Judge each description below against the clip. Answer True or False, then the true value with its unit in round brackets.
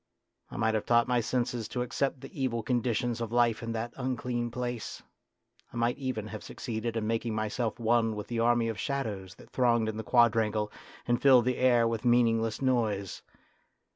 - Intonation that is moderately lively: False (1.7 semitones)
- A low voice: True (115 Hz)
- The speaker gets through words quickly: False (185 wpm)